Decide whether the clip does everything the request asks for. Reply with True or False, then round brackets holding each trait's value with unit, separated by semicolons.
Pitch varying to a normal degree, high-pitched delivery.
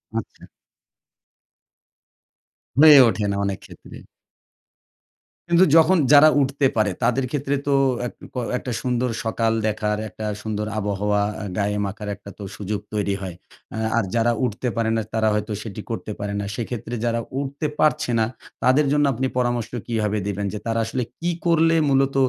False (4.3 semitones; 115 Hz)